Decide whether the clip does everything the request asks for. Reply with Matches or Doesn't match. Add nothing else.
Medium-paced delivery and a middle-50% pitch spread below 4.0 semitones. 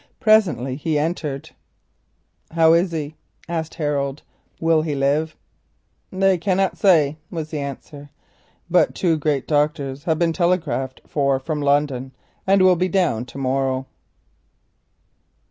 Doesn't match